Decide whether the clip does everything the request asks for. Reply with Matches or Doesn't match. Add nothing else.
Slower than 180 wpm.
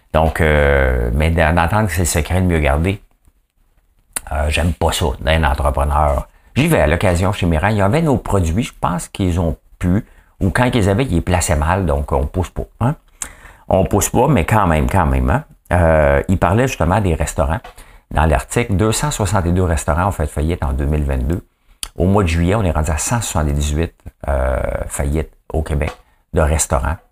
Doesn't match